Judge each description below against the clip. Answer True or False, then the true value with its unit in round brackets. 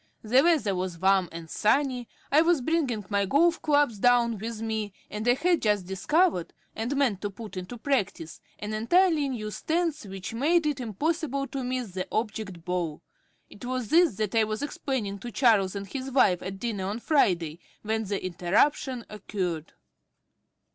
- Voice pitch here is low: False (220 Hz)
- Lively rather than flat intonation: True (5.9 semitones)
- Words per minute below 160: False (170 wpm)